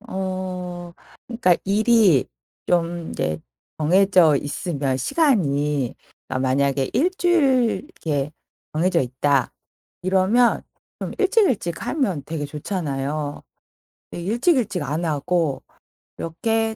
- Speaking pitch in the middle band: Yes, medium, 175 Hz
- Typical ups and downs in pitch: No, wide, 7.2 semitones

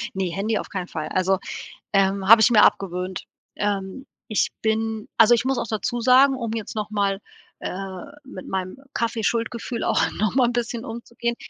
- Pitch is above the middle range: Yes, high, 215 Hz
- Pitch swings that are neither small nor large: Yes, average, 3.5 semitones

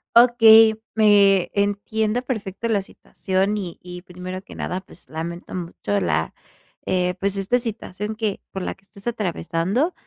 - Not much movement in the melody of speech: No, average, 3.3 semitones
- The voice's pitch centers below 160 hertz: No, high, 195 Hz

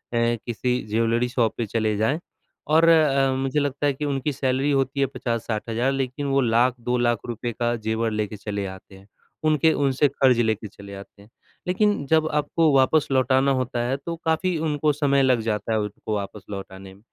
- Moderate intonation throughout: Yes, average, 4.2 semitones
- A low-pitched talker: Yes, low, 125 Hz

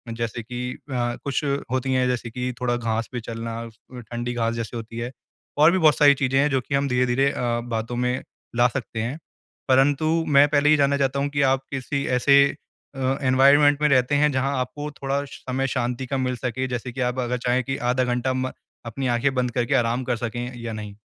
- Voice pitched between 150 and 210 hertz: No, low, 125 Hz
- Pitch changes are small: Yes, narrow, 2.2 semitones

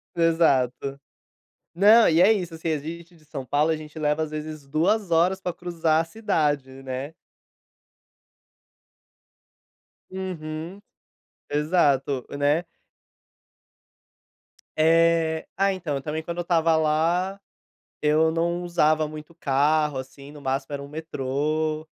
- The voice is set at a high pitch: No, medium, 155 Hz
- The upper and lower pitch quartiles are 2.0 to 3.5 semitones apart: Yes, narrow, 2.4 semitones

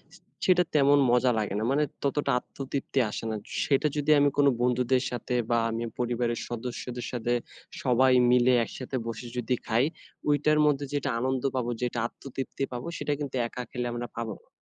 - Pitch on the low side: Yes, low, 125 Hz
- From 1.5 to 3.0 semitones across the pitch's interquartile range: Yes, narrow, 2.4 semitones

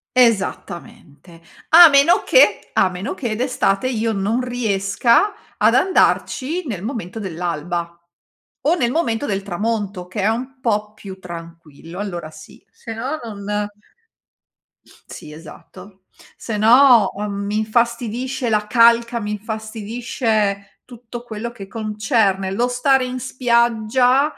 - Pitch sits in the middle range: No, high, 220 Hz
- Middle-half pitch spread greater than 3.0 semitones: Yes, average, 3.9 semitones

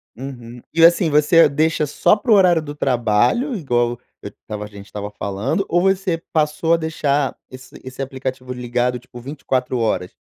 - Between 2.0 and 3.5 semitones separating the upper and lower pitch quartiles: No, average, 5.0 semitones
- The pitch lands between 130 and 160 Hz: Yes, low, 135 Hz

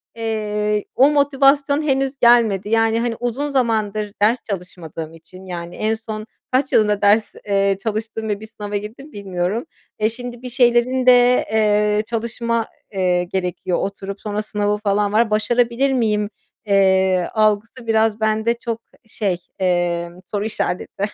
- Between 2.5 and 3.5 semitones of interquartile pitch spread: Yes, average, 2.9 semitones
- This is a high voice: Yes, high, 215 Hz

